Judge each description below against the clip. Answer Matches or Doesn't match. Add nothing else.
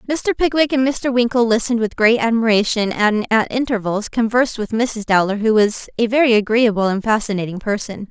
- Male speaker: Doesn't match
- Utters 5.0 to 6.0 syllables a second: Matches